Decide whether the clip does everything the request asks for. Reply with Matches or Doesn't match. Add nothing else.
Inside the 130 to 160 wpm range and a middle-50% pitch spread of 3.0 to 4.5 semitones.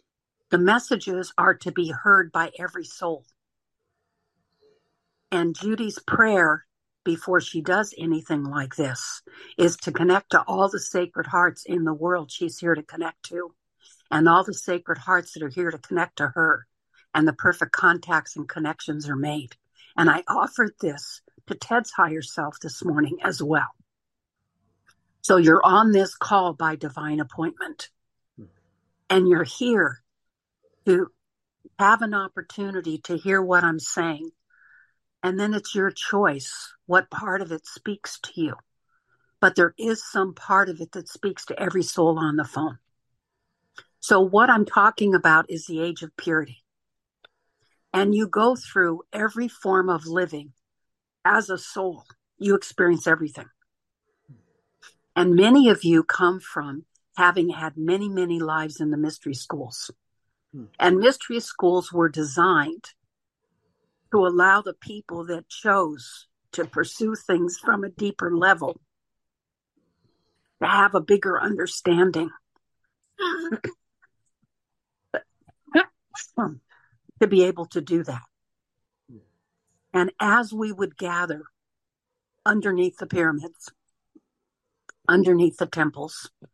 Matches